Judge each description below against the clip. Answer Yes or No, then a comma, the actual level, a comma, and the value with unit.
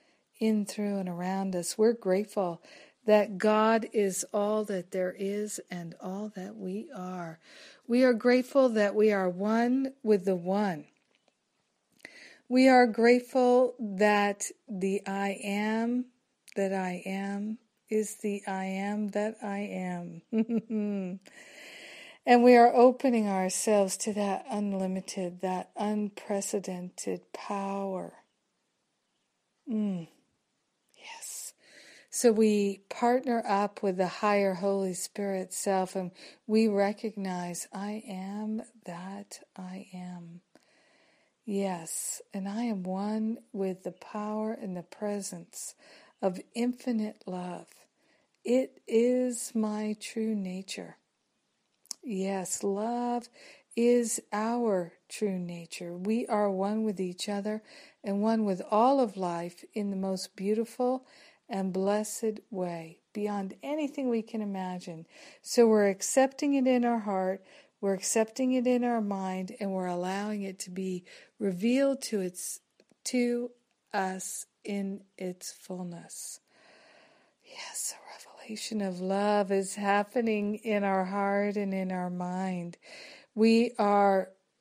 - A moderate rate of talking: No, slow, 120 wpm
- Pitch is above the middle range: Yes, high, 205 Hz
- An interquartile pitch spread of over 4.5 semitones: No, average, 3.3 semitones